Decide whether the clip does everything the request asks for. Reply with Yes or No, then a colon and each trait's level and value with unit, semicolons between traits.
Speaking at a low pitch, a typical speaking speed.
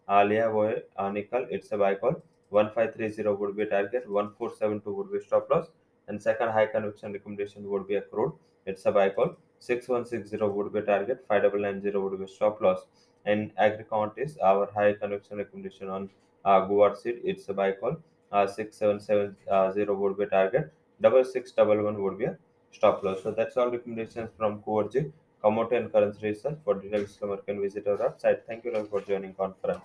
Yes: low, 105 Hz; average, 190 wpm